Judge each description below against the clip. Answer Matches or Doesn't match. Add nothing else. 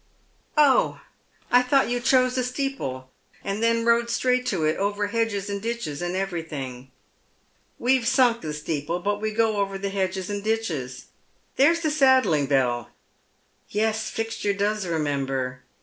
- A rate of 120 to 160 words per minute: Matches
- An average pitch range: Doesn't match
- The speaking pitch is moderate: Doesn't match